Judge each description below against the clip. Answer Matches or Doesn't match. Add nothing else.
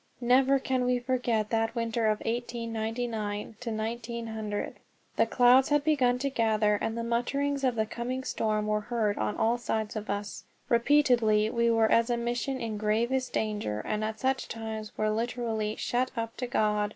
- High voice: Matches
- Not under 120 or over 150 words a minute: Doesn't match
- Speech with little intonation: Matches